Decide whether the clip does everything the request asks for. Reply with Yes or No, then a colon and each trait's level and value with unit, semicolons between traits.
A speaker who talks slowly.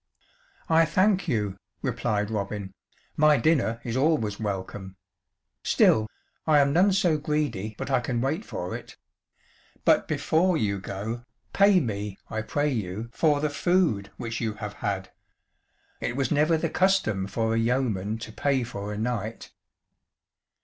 No: average, 150 wpm